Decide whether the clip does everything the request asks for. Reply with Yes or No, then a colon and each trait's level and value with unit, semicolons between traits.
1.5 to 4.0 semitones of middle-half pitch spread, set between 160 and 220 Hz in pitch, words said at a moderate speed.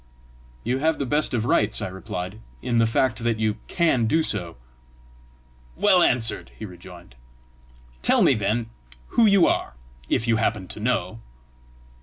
No: average, 3.7 semitones; low, 115 Hz; average, 155 wpm